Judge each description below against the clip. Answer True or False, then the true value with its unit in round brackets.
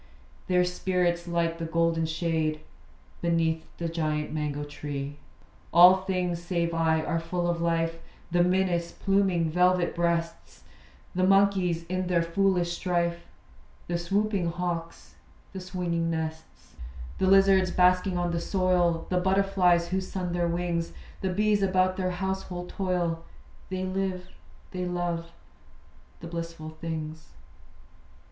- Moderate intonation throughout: False (1.7 semitones)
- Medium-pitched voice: True (175 Hz)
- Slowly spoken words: True (130 wpm)